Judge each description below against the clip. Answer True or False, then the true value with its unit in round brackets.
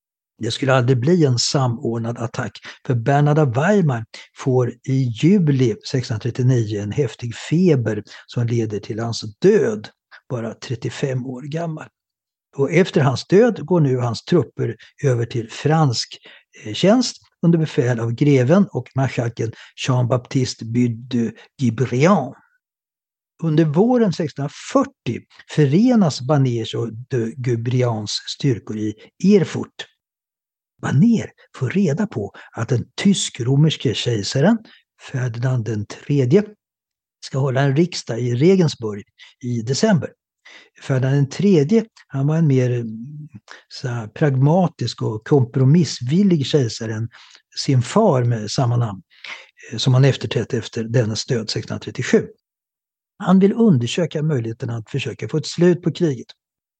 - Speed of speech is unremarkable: False (115 wpm)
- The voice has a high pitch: False (135 Hz)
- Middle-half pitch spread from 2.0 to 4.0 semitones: False (5.1 semitones)